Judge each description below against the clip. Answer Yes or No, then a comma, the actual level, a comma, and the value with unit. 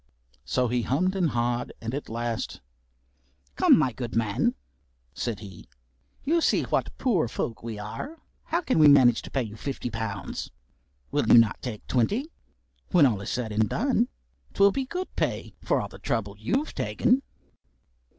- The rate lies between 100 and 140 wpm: No, average, 170 wpm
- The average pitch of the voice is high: No, low, 120 Hz